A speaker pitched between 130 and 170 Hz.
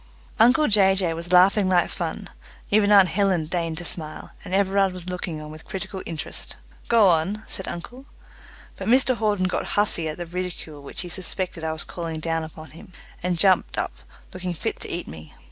No: medium, 180 Hz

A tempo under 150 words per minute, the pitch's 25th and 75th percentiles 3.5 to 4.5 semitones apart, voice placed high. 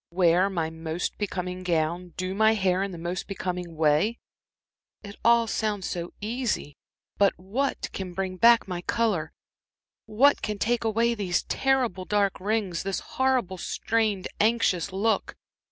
Yes: average, 140 wpm; average, 3.8 semitones; high, 195 Hz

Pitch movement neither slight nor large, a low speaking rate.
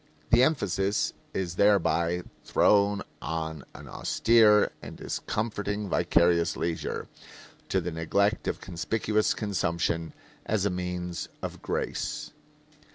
Yes: average, 3.5 semitones; slow, 105 wpm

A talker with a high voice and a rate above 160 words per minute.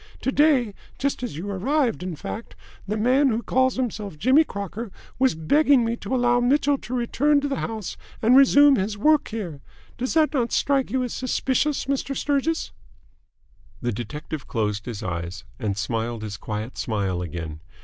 Yes: high, 235 Hz; average, 170 wpm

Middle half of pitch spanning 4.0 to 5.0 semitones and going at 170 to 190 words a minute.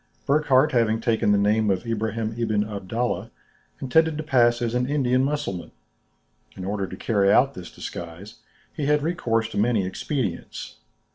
No: average, 4.5 semitones; average, 155 wpm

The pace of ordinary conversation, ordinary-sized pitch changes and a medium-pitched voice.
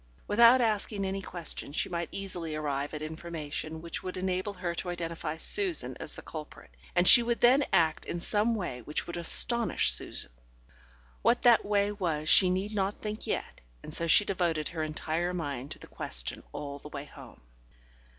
Yes: average, 180 wpm; average, 4.8 semitones; medium, 175 Hz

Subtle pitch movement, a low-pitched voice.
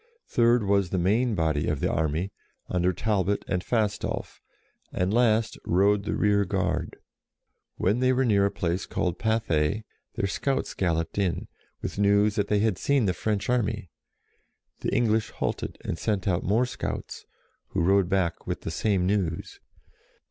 No: average, 3.3 semitones; low, 100 Hz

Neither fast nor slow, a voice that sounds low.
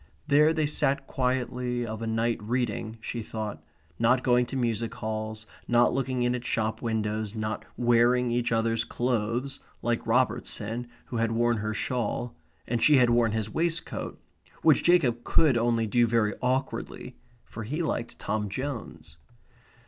Yes: average, 155 wpm; low, 120 Hz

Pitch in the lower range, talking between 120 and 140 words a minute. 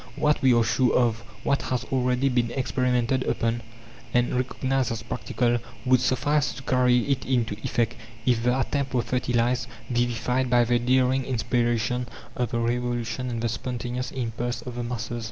No: low, 125 Hz; average, 165 wpm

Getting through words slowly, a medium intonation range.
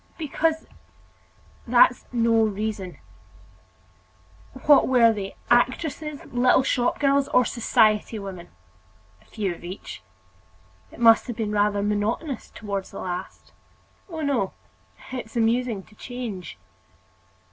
Yes: slow, 115 wpm; average, 3.8 semitones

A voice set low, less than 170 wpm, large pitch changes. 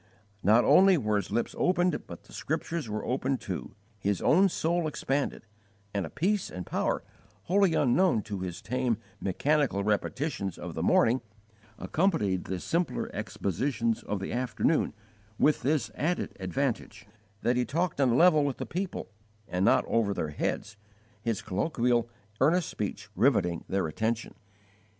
Yes: low, 125 Hz; average, 150 wpm; wide, 7.5 semitones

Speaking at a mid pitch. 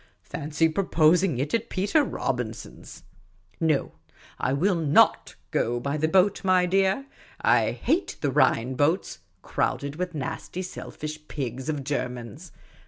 Yes: medium, 155 Hz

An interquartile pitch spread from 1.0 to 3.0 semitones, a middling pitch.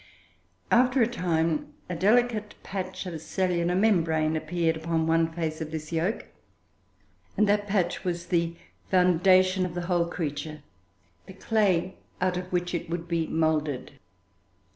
Yes: narrow, 2.5 semitones; medium, 175 Hz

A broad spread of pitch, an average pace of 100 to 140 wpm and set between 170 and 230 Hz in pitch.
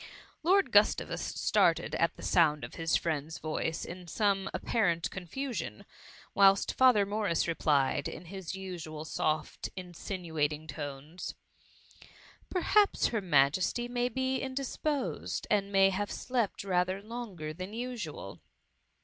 Yes: wide, 6.1 semitones; slow, 135 wpm; medium, 185 Hz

